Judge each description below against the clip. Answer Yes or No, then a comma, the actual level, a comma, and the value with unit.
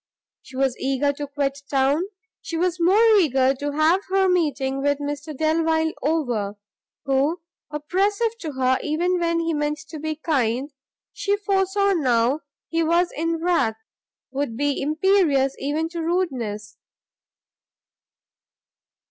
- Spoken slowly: Yes, slow, 130 wpm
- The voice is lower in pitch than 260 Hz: No, very high, 300 Hz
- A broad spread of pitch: No, average, 3.9 semitones